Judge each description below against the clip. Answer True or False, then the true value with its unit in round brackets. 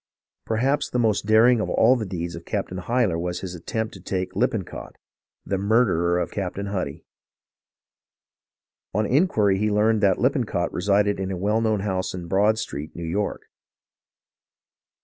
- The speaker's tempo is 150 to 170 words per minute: True (160 wpm)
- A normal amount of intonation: True (3.2 semitones)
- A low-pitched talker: True (100 Hz)